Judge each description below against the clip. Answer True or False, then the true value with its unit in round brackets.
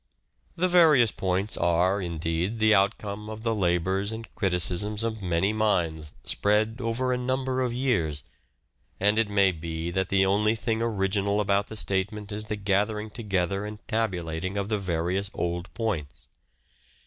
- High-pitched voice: False (100 Hz)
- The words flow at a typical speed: True (155 wpm)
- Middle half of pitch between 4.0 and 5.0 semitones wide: False (3.3 semitones)